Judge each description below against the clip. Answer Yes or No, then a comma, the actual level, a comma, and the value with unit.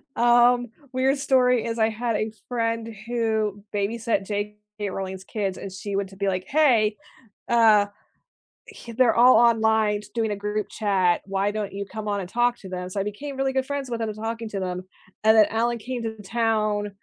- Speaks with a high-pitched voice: Yes, high, 220 Hz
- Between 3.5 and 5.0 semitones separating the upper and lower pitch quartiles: No, average, 2.7 semitones